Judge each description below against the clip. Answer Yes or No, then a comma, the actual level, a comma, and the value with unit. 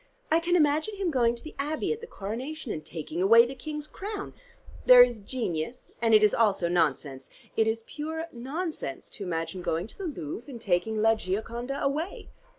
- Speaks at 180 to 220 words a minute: Yes, average, 190 wpm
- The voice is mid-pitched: No, high, 235 Hz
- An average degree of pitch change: No, wide, 7.6 semitones